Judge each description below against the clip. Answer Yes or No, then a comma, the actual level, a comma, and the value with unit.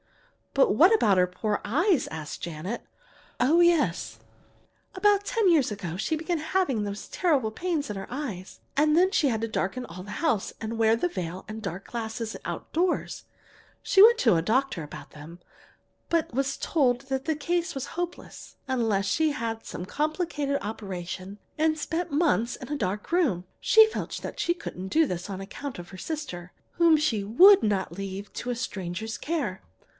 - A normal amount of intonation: No, wide, 8.4 semitones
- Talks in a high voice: Yes, high, 245 Hz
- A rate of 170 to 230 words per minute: Yes, average, 180 wpm